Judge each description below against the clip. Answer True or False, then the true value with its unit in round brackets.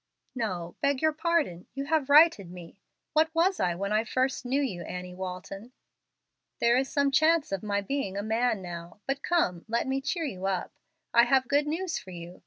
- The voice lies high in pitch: True (240 Hz)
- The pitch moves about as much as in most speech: False (7.4 semitones)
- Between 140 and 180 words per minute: False (195 wpm)